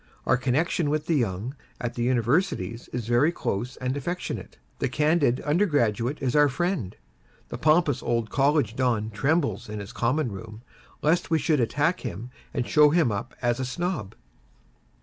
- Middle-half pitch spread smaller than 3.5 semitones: No, average, 4.6 semitones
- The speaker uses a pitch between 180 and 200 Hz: No, low, 130 Hz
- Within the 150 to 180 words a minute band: Yes, average, 165 wpm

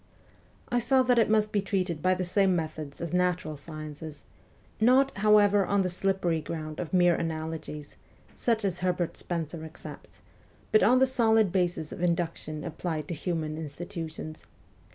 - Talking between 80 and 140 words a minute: No, average, 155 wpm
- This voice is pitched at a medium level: Yes, medium, 175 Hz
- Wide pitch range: No, average, 4.2 semitones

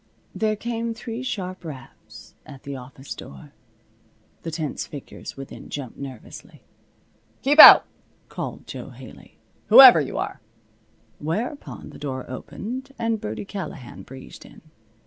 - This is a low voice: No, medium, 160 Hz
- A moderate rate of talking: No, slow, 125 wpm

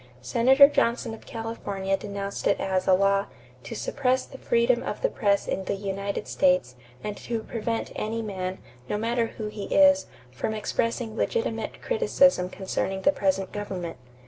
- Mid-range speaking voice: No, high, 210 Hz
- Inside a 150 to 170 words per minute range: Yes, average, 160 wpm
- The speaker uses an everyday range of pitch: Yes, average, 3.5 semitones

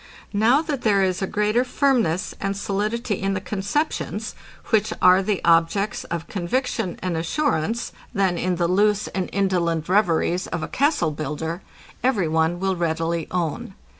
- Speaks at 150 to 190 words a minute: Yes, average, 155 wpm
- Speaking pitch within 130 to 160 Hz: No, high, 190 Hz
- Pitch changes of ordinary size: Yes, average, 3.9 semitones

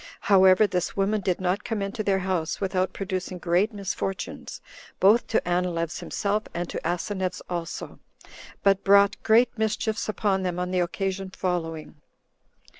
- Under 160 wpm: Yes, average, 145 wpm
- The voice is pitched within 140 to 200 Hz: Yes, high, 190 Hz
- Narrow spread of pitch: Yes, narrow, 2.1 semitones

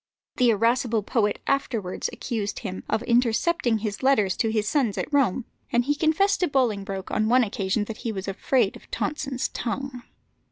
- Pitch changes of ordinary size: Yes, average, 4.1 semitones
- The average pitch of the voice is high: Yes, high, 230 Hz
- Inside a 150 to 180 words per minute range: Yes, average, 170 wpm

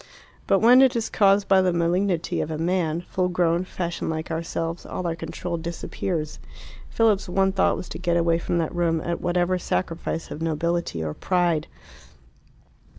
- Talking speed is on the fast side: No, average, 170 wpm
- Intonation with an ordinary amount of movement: No, narrow, 2.0 semitones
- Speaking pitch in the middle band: Yes, medium, 175 Hz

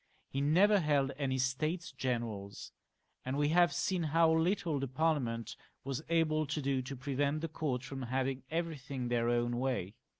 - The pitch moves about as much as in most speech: Yes, average, 3.8 semitones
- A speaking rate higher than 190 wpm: No, average, 165 wpm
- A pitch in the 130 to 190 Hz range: Yes, medium, 140 Hz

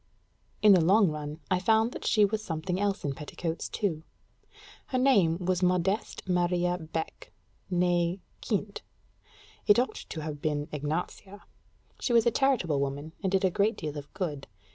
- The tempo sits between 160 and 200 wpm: Yes, average, 165 wpm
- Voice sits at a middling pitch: Yes, medium, 180 Hz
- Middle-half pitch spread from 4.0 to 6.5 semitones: Yes, average, 4.4 semitones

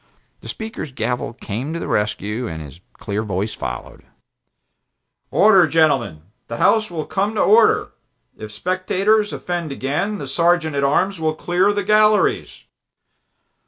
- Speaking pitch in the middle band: Yes, medium, 160 Hz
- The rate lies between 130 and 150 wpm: Yes, average, 140 wpm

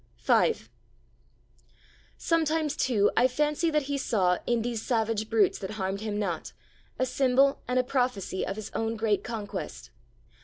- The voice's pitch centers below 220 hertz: No, high, 230 Hz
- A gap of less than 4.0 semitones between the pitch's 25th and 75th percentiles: No, average, 4.5 semitones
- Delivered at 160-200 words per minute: No, average, 150 wpm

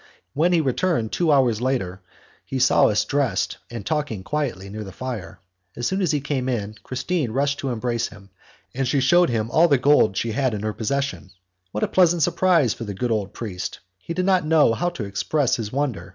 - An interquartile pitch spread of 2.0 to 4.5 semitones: No, wide, 5.5 semitones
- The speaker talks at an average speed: No, fast, 210 wpm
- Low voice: Yes, low, 125 Hz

